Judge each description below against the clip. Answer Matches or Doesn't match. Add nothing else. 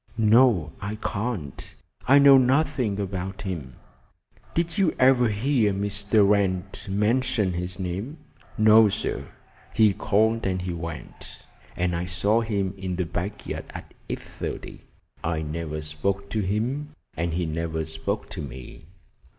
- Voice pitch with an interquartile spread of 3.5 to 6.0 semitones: Matches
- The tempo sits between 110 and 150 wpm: Matches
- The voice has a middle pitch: Doesn't match